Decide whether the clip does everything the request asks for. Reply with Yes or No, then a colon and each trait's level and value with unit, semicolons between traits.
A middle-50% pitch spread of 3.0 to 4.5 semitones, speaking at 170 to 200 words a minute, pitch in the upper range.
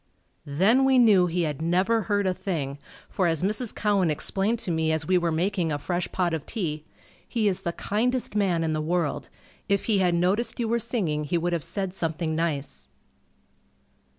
No: average, 4.2 semitones; average, 195 wpm; medium, 180 Hz